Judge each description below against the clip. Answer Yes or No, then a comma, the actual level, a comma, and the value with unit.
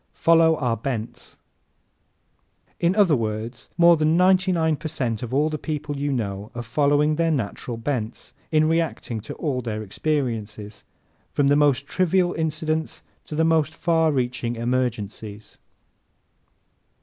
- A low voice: No, medium, 145 Hz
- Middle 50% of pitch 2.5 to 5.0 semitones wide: No, wide, 5.5 semitones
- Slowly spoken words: No, average, 145 wpm